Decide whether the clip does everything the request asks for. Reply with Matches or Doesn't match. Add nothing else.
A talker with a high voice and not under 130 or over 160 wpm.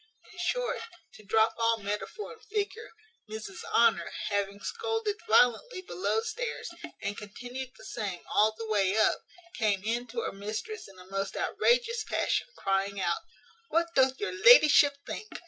Matches